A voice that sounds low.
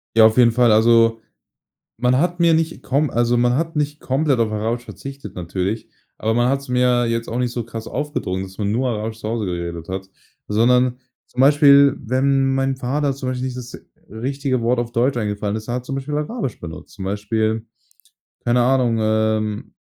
Yes: low, 120 Hz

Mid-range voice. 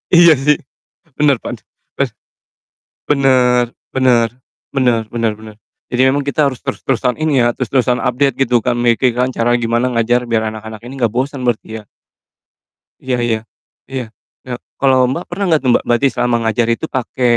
No: low, 125 Hz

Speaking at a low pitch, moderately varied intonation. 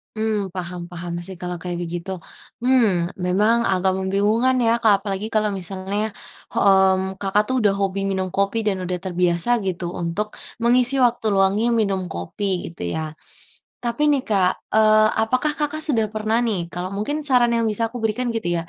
No: high, 200 Hz; average, 3.3 semitones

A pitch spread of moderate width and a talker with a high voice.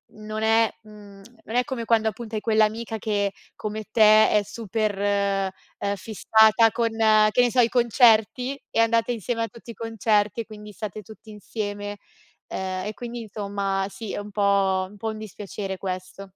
No: narrow, 2.0 semitones; high, 215 Hz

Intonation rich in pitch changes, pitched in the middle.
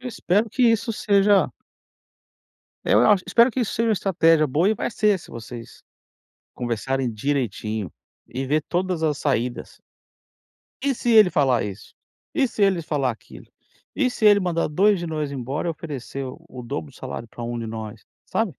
Yes: wide, 8.5 semitones; medium, 155 Hz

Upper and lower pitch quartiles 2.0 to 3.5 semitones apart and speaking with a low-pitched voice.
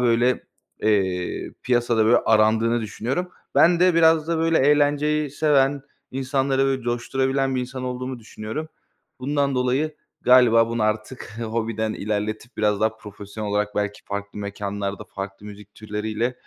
No: average, 4.0 semitones; low, 120 Hz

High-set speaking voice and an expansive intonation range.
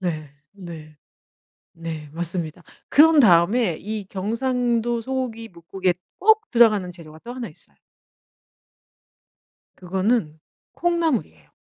Yes: high, 195 Hz; wide, 6.3 semitones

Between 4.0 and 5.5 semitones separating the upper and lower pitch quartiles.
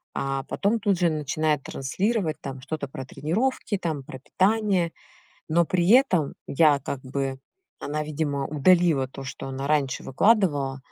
Yes: average, 4.8 semitones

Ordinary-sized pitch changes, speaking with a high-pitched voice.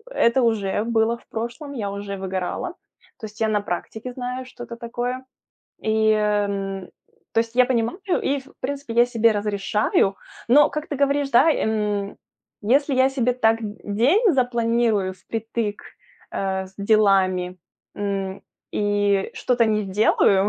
Yes: average, 3.6 semitones; high, 225 Hz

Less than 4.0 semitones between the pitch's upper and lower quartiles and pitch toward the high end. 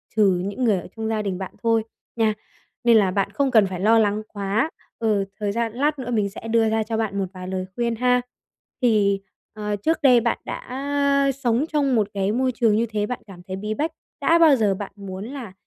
Yes: average, 3.4 semitones; high, 220 Hz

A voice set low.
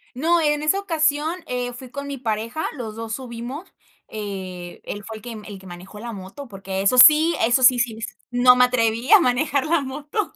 No: high, 245 Hz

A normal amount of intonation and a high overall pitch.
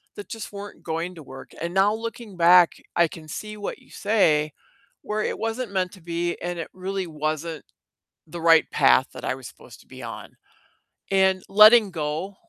No: average, 3.9 semitones; medium, 180 Hz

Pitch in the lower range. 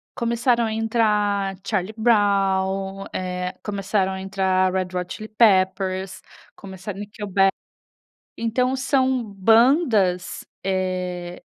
No: high, 195 Hz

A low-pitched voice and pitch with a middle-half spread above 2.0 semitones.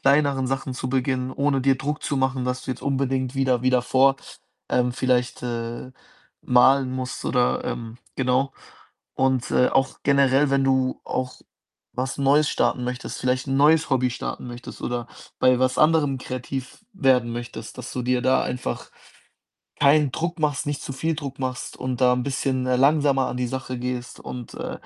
No: low, 130 Hz; narrow, 1.5 semitones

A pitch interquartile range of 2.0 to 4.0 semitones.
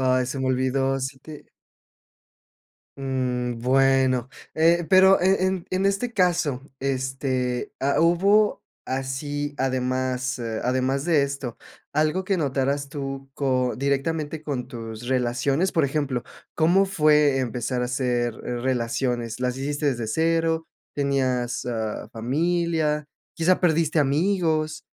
Yes: average, 3.7 semitones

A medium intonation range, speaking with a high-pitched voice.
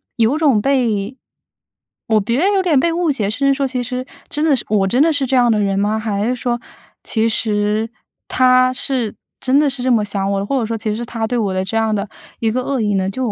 Yes: average, 3.8 semitones; high, 235 Hz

